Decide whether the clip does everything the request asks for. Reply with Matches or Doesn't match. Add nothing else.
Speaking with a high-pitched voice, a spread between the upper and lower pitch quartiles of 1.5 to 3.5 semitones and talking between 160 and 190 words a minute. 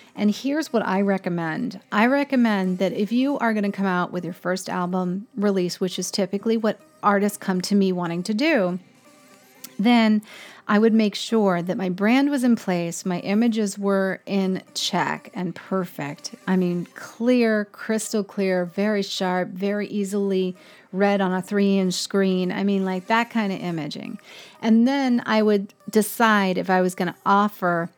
Matches